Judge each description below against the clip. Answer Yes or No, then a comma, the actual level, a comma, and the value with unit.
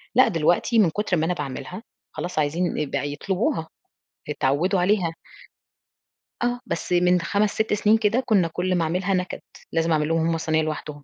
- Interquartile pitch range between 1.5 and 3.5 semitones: No, average, 4.2 semitones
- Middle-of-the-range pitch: Yes, medium, 175 Hz